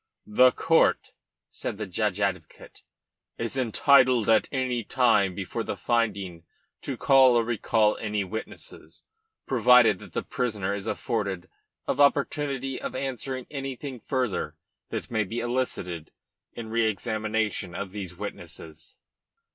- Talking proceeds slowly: Yes, slow, 130 wpm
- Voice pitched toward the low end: Yes, low, 110 Hz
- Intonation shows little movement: No, average, 4.1 semitones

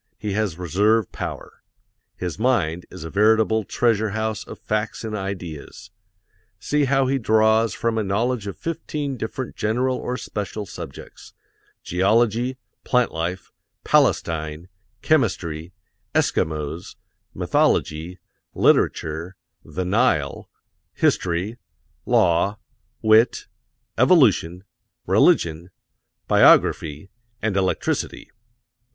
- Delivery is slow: Yes, slow, 95 wpm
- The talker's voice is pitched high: No, low, 105 Hz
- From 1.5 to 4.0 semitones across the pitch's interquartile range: No, average, 4.6 semitones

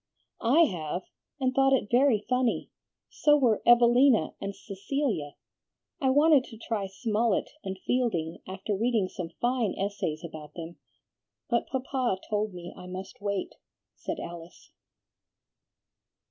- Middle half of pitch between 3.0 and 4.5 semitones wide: No, average, 5.3 semitones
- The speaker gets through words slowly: Yes, slow, 130 wpm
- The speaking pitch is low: No, high, 215 Hz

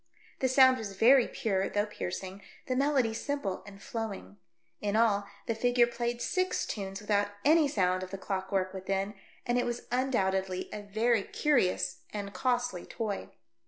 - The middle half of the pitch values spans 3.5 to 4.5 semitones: Yes, average, 4.1 semitones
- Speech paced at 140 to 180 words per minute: Yes, average, 160 wpm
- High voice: Yes, high, 210 Hz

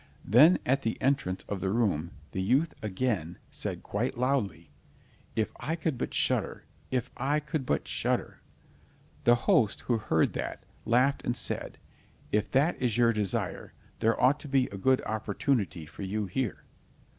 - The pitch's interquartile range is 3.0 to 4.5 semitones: No, average, 5.0 semitones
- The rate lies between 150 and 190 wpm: Yes, average, 160 wpm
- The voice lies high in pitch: No, low, 120 Hz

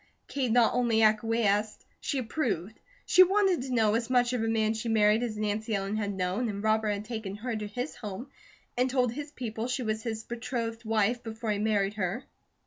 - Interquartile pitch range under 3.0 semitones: Yes, narrow, 2.5 semitones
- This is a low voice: No, high, 225 Hz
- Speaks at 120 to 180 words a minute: No, fast, 205 wpm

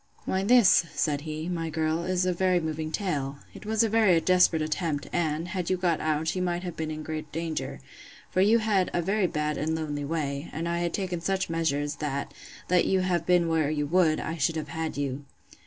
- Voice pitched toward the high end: No, medium, 165 Hz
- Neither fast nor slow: No, fast, 220 wpm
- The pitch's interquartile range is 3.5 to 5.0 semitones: No, average, 2.8 semitones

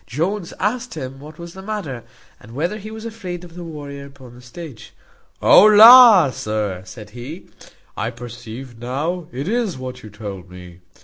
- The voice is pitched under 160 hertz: Yes, medium, 140 Hz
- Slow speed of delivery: No, average, 175 wpm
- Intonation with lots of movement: Yes, wide, 7.5 semitones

